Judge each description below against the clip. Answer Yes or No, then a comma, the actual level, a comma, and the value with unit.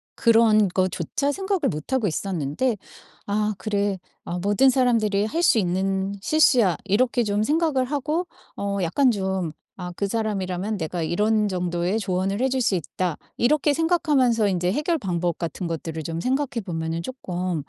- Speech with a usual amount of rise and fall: No, wide, 6.0 semitones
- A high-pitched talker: Yes, high, 205 Hz